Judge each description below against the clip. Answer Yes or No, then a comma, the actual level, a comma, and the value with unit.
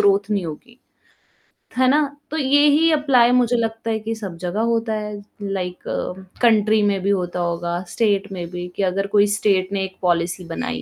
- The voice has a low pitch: No, high, 205 Hz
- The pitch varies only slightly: No, average, 3.6 semitones